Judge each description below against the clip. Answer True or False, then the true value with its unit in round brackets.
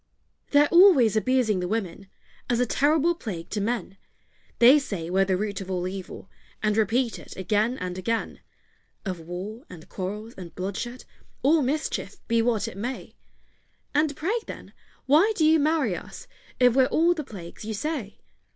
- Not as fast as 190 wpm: True (170 wpm)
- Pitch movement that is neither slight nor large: False (6.6 semitones)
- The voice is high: True (225 Hz)